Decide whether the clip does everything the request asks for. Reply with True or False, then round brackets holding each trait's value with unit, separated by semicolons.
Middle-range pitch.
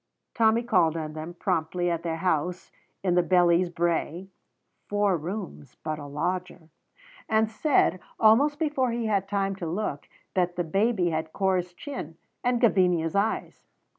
True (180 Hz)